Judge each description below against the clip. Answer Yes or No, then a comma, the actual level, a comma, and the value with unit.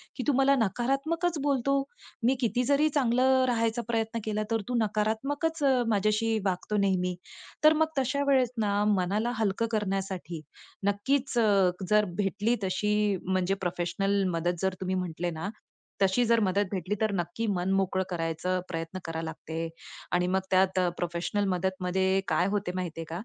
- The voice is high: Yes, high, 200 Hz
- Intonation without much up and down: No, average, 4.3 semitones